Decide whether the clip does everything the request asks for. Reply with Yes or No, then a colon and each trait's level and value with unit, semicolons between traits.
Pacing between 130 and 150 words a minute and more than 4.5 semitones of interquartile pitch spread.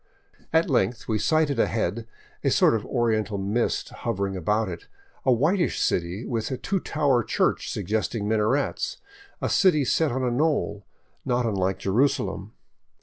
Yes: average, 145 wpm; average, 5.0 semitones